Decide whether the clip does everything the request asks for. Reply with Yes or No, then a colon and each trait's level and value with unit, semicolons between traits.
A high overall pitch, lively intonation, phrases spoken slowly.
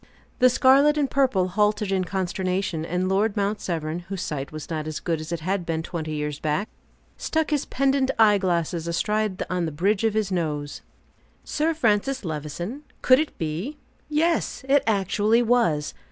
No: high, 195 Hz; wide, 6.4 semitones; average, 170 wpm